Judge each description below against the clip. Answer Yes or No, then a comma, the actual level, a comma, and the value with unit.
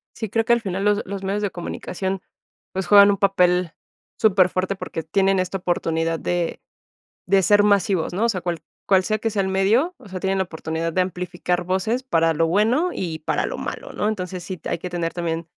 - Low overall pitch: No, high, 190 Hz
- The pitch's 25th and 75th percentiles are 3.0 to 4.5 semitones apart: No, narrow, 2.5 semitones